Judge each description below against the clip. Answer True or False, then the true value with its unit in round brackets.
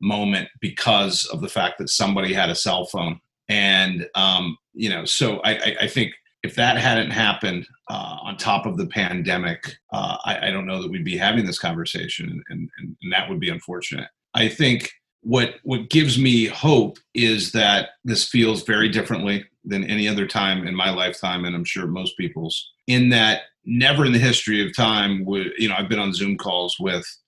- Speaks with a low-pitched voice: True (110 Hz)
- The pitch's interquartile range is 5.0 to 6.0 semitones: False (4.2 semitones)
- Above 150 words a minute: True (200 wpm)